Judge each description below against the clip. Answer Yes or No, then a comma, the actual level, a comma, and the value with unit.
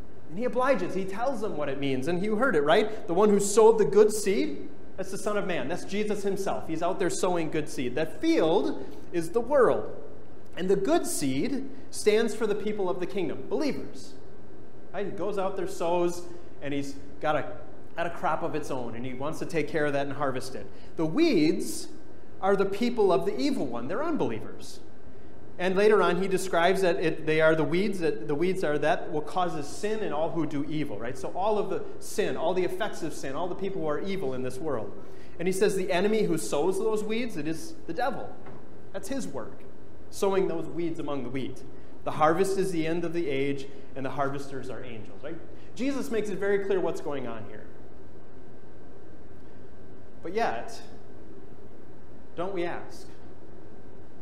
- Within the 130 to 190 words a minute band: No, fast, 205 wpm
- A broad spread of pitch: Yes, wide, 5.9 semitones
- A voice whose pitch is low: No, medium, 175 Hz